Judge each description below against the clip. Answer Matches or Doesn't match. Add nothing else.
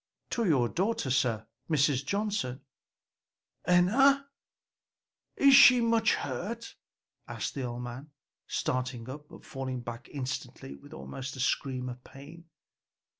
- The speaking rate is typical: Doesn't match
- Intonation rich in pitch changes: Matches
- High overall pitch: Doesn't match